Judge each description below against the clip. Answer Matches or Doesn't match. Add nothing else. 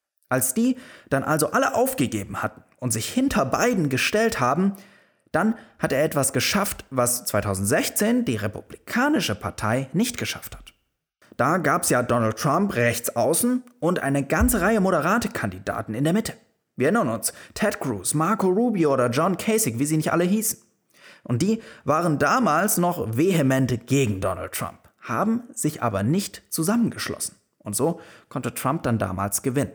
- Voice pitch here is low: Doesn't match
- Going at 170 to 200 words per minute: Doesn't match